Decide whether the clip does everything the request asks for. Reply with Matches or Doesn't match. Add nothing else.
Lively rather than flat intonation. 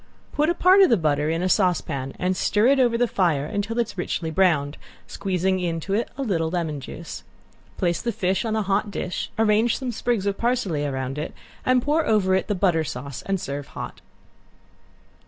Matches